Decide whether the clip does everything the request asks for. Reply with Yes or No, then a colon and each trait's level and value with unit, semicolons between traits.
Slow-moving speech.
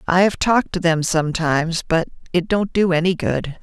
No: average, 200 wpm